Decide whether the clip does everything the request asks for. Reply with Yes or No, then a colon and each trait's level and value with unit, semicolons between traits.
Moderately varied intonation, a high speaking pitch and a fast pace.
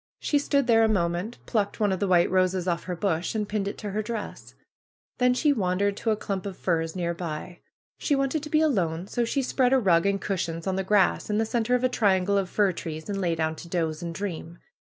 Yes: average, 4.3 semitones; high, 195 Hz; fast, 245 wpm